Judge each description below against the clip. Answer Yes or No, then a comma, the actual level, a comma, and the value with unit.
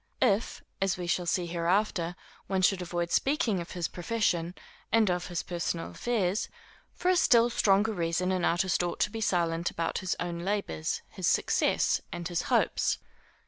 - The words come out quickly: No, average, 170 wpm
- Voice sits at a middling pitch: Yes, medium, 180 Hz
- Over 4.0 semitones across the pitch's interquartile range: No, average, 3.1 semitones